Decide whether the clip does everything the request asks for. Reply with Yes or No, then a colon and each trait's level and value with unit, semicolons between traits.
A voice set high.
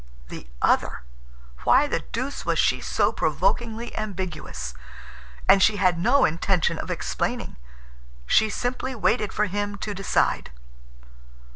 Yes: high, 205 Hz